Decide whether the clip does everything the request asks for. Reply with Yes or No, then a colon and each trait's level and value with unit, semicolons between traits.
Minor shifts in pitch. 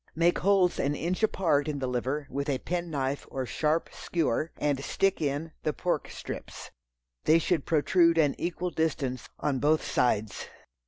No: average, 3.4 semitones